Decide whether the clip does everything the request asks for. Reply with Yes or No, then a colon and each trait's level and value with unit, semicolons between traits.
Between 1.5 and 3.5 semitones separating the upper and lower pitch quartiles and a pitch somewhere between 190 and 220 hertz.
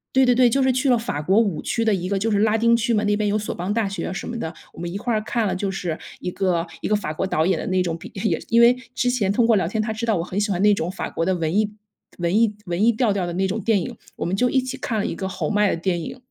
No: average, 3.9 semitones; high, 205 Hz